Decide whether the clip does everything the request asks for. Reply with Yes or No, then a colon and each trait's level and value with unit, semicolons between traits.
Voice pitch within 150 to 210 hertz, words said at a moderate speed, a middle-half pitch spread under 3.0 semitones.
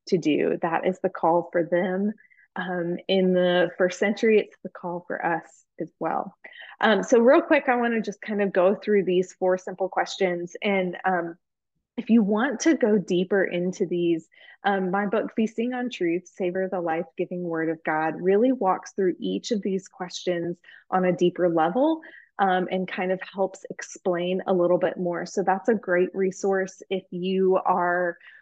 Yes: medium, 185 Hz; average, 185 wpm; narrow, 2.4 semitones